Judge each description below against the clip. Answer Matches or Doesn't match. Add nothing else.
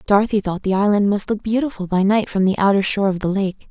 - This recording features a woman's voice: Matches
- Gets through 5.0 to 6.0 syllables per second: Doesn't match